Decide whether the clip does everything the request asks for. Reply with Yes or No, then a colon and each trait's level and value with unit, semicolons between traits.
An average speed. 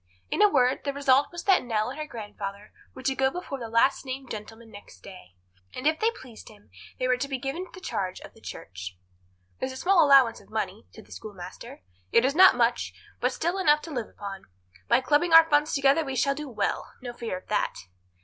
No: fast, 225 wpm